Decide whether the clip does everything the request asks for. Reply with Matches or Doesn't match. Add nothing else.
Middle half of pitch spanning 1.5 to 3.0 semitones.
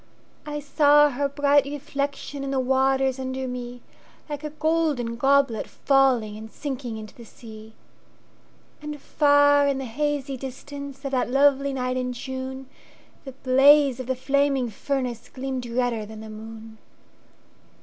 Matches